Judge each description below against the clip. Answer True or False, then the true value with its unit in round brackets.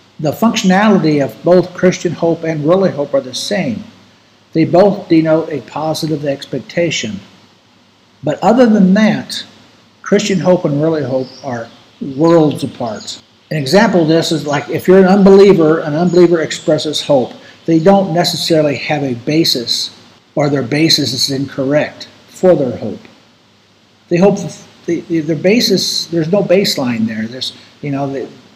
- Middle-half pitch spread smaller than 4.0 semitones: False (4.5 semitones)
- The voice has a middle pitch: True (165 Hz)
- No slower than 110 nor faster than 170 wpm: True (150 wpm)